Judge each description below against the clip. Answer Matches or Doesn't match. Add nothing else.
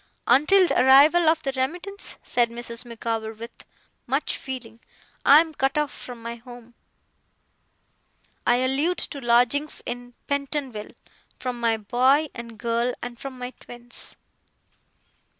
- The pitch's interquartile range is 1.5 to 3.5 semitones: Matches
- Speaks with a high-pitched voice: Matches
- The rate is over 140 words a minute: Doesn't match